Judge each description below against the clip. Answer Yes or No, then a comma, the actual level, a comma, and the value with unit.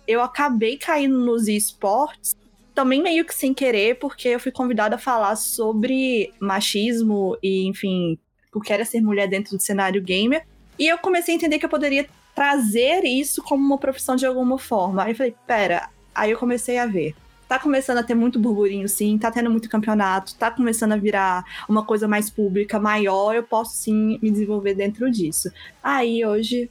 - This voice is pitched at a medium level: No, high, 225 Hz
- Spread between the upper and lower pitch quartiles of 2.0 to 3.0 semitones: No, average, 3.8 semitones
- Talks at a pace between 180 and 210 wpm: Yes, fast, 185 wpm